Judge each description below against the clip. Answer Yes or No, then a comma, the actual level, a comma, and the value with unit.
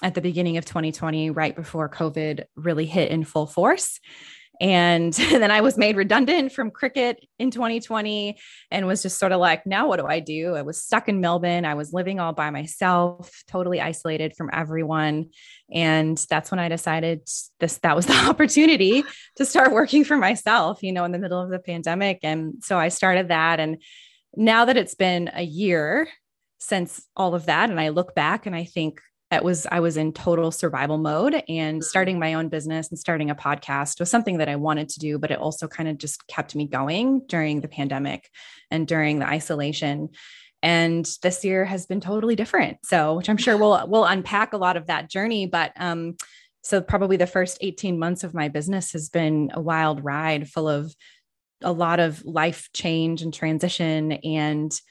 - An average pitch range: Yes, average, 3.4 semitones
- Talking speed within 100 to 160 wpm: No, average, 195 wpm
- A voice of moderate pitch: Yes, medium, 170 Hz